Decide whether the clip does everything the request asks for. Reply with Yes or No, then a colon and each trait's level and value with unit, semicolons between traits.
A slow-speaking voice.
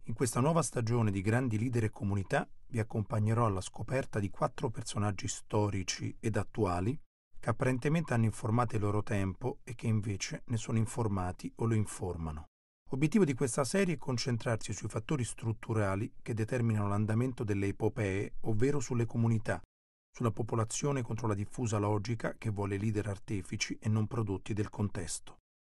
No: average, 155 wpm